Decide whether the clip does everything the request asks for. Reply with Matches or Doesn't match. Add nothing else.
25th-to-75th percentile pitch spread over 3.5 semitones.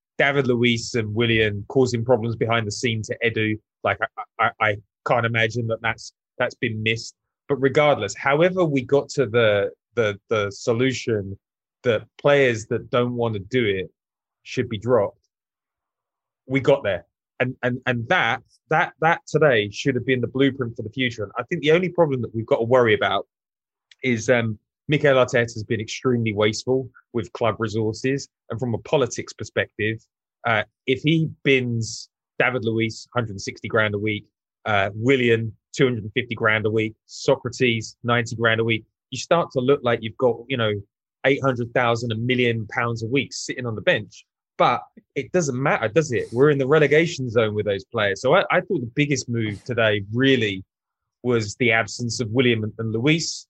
Doesn't match